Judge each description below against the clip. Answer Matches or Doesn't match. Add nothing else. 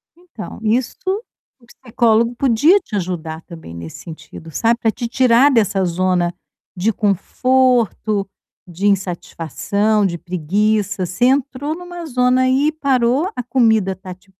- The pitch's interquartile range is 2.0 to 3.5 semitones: Doesn't match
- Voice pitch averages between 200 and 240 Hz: Matches